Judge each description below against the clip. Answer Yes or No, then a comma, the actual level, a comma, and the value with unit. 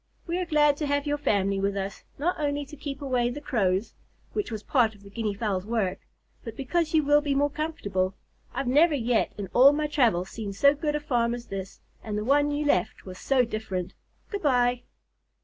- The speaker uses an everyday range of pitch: No, wide, 6.1 semitones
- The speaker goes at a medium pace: No, fast, 215 wpm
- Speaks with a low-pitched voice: No, very high, 250 Hz